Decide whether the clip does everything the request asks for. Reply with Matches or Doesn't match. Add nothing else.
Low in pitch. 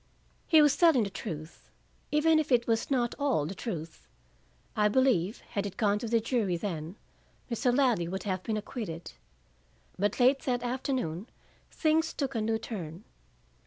Doesn't match